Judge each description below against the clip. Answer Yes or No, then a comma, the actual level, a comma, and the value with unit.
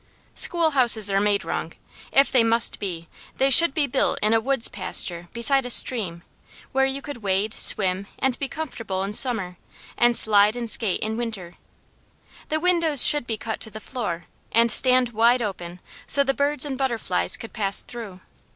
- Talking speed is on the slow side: No, average, 180 wpm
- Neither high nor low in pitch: No, high, 230 Hz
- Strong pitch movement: No, average, 5.0 semitones